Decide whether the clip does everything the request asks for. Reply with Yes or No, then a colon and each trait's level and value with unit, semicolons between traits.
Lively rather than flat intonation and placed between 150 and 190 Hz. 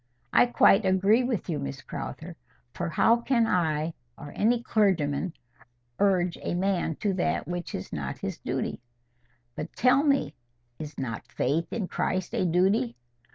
Yes: wide, 5.7 semitones; medium, 185 Hz